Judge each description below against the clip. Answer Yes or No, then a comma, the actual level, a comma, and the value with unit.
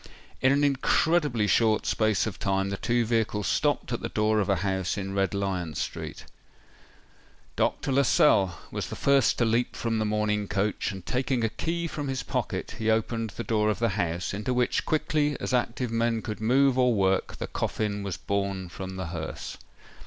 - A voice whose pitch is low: Yes, low, 110 Hz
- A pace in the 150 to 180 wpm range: No, average, 190 wpm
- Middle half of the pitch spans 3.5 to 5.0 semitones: Yes, average, 4.0 semitones